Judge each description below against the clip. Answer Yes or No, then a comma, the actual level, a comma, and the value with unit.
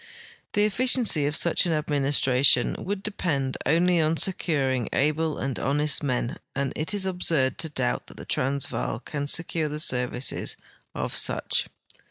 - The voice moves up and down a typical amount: Yes, average, 4.1 semitones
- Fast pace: No, average, 150 wpm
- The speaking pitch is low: No, medium, 150 Hz